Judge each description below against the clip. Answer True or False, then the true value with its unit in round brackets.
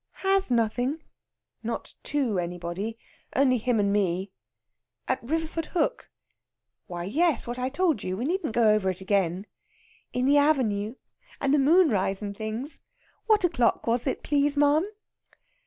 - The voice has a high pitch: True (245 Hz)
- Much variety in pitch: True (6.4 semitones)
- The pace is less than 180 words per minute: True (140 wpm)